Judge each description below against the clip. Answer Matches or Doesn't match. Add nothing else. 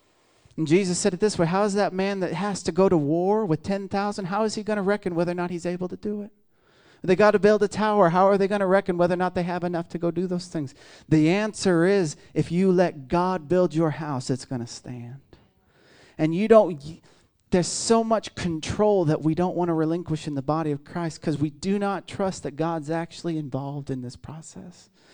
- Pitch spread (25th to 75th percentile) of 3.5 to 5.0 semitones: Matches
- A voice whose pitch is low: Doesn't match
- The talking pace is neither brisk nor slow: Doesn't match